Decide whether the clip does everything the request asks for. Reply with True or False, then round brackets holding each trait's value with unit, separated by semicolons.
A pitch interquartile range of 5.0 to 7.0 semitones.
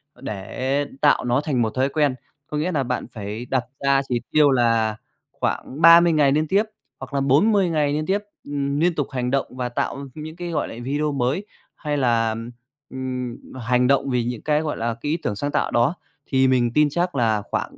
False (3.8 semitones)